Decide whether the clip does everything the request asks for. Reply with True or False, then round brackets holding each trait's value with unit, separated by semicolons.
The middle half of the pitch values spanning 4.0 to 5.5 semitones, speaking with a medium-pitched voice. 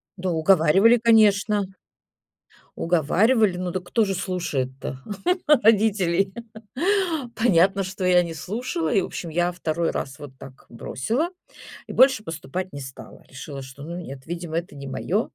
True (4.4 semitones; 180 Hz)